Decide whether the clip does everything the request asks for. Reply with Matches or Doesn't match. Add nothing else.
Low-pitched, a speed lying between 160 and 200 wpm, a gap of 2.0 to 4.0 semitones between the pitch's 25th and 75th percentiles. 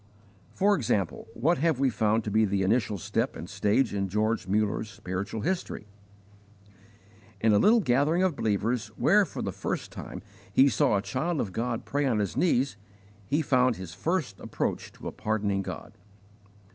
Doesn't match